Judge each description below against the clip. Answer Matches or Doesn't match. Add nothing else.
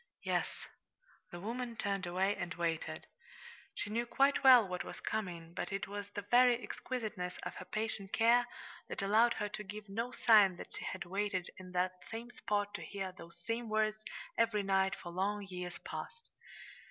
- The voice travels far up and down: Doesn't match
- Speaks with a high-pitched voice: Matches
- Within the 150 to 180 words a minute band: Matches